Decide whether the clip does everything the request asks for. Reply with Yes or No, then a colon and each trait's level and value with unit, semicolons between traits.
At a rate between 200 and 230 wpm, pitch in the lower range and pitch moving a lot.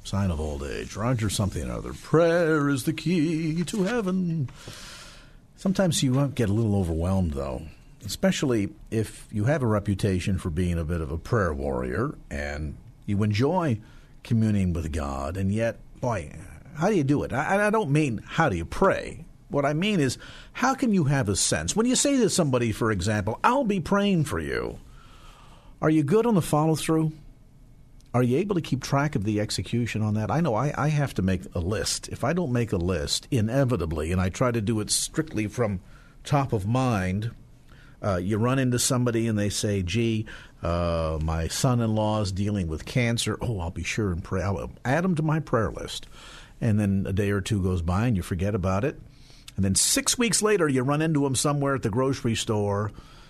Yes: fast, 205 wpm; low, 115 Hz; wide, 6.6 semitones